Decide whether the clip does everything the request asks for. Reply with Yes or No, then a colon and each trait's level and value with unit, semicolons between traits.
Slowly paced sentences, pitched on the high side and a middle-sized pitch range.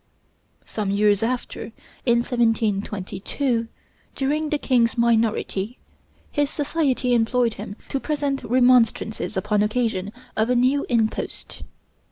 Yes: slow, 110 wpm; high, 235 Hz; average, 3.1 semitones